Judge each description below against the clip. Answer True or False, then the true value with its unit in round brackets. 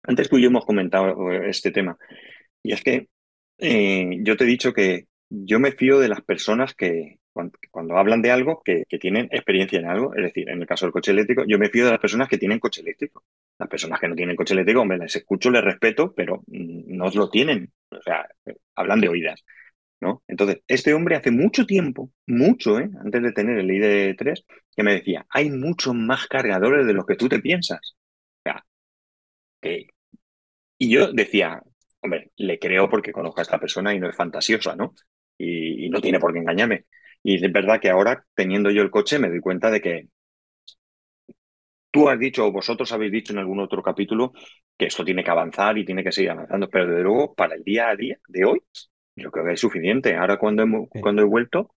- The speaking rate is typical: False (210 wpm)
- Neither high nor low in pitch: False (105 Hz)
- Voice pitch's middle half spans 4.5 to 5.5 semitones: True (5.2 semitones)